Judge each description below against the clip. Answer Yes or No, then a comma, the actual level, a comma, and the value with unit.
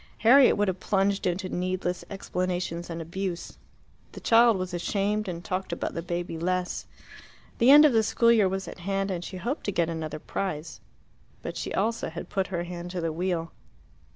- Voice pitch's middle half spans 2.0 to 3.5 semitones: Yes, narrow, 2.6 semitones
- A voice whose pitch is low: No, medium, 185 Hz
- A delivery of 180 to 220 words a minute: Yes, average, 190 wpm